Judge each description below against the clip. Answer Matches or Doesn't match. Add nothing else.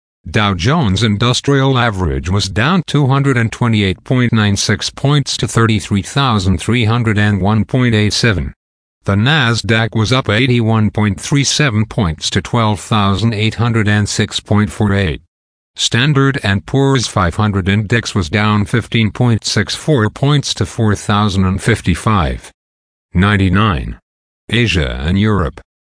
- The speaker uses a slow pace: Matches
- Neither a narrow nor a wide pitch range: Matches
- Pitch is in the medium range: Doesn't match